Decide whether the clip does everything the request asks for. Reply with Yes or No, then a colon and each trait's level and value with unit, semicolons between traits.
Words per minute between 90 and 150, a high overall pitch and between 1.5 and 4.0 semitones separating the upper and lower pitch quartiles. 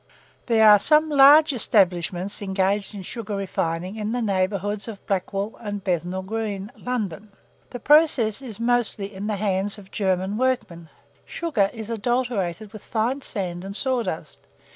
Yes: average, 145 wpm; high, 205 Hz; average, 3.4 semitones